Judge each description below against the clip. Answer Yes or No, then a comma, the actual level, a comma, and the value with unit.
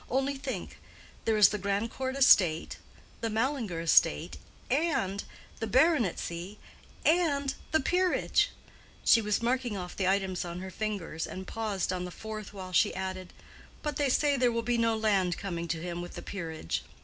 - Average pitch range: No, wide, 5.7 semitones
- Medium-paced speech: Yes, average, 160 wpm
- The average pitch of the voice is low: No, high, 210 Hz